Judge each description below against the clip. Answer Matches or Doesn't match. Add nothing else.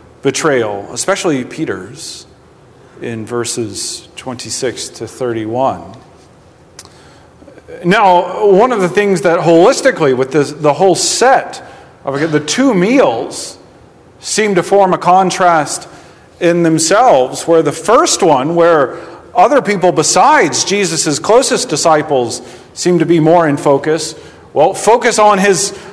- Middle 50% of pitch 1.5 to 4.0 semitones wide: Doesn't match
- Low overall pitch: Doesn't match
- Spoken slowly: Matches